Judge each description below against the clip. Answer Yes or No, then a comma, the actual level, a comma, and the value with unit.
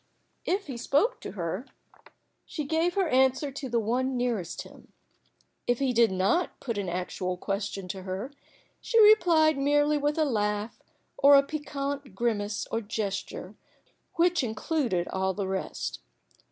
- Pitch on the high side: Yes, very high, 250 Hz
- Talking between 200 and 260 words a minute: No, average, 155 wpm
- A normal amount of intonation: No, wide, 6.3 semitones